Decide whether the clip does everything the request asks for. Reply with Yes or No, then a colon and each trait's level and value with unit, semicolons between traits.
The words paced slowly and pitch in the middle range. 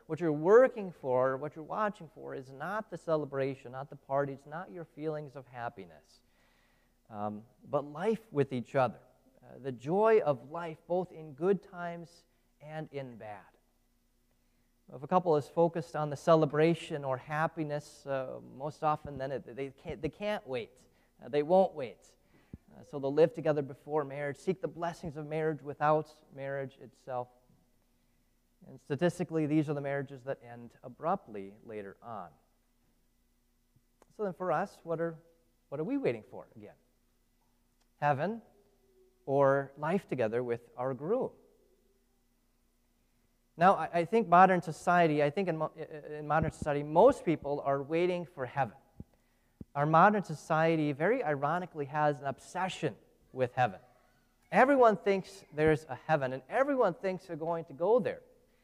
No: average, 150 wpm; medium, 150 Hz